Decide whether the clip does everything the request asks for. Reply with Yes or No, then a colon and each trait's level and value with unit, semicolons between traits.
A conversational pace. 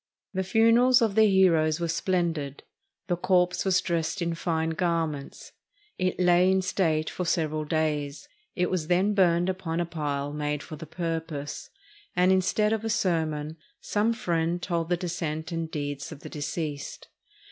Yes: average, 160 wpm